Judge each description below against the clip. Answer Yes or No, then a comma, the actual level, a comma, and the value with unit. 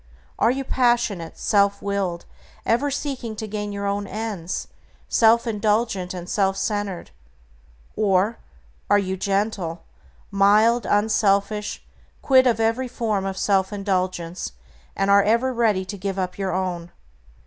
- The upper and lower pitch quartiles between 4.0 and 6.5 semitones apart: No, average, 2.8 semitones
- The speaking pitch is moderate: No, high, 200 Hz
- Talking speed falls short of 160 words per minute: Yes, slow, 135 wpm